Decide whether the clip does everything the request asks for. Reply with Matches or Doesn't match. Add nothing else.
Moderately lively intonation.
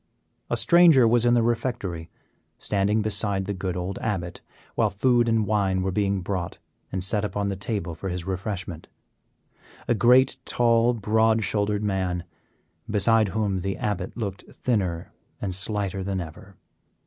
Matches